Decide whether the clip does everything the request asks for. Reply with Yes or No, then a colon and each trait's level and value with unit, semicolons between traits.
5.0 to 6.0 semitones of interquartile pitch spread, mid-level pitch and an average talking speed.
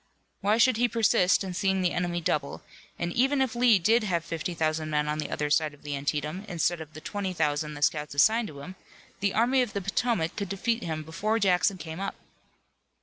No: wide, 5.5 semitones; medium, 180 Hz; fast, 215 wpm